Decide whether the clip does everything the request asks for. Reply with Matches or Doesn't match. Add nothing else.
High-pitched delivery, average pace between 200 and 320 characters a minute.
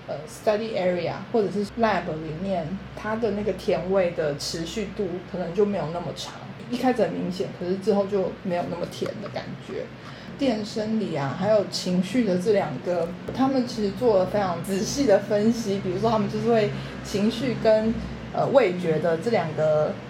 Matches